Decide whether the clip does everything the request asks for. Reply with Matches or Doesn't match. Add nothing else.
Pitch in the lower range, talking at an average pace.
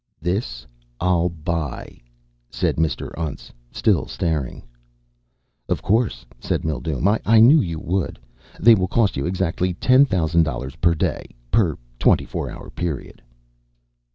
Doesn't match